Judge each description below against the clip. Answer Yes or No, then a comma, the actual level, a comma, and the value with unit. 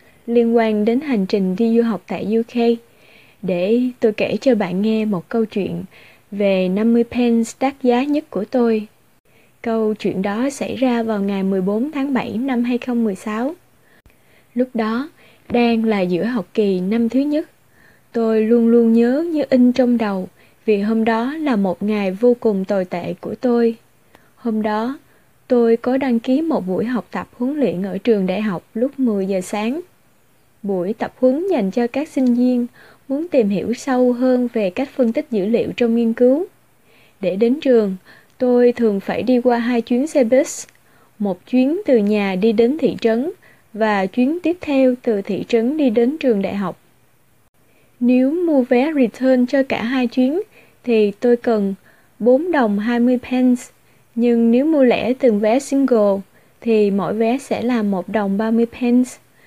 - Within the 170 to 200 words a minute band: Yes, average, 175 wpm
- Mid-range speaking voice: No, high, 235 Hz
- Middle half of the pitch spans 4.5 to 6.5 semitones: No, average, 3.0 semitones